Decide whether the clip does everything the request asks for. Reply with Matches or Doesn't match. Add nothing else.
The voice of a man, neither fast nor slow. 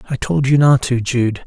Doesn't match